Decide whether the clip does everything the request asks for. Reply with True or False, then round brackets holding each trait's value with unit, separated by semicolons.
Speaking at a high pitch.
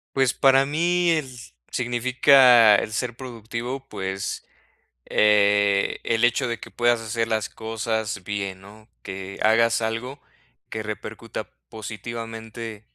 False (115 Hz)